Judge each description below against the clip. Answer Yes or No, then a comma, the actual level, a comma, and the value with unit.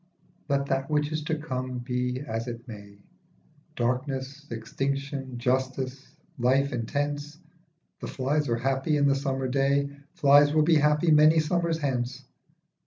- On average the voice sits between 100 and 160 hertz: Yes, low, 135 Hz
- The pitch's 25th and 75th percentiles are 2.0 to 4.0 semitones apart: Yes, narrow, 2.5 semitones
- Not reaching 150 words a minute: Yes, average, 140 wpm